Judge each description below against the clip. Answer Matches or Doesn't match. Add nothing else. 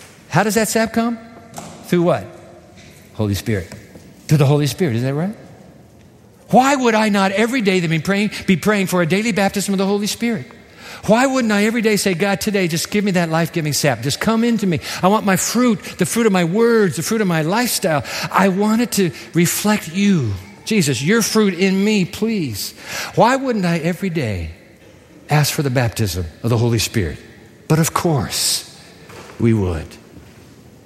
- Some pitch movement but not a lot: Doesn't match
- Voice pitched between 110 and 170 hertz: Doesn't match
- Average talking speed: Matches